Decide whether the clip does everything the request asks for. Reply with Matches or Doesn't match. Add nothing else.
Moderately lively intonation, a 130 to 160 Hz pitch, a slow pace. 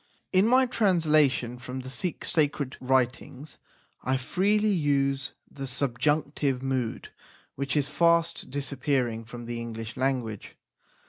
Matches